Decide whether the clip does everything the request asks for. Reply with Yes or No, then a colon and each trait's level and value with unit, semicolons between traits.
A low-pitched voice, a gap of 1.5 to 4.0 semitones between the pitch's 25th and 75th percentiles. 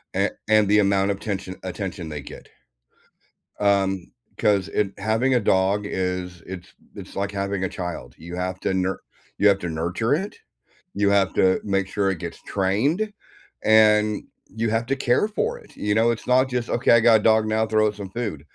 Yes: low, 100 Hz; average, 2.8 semitones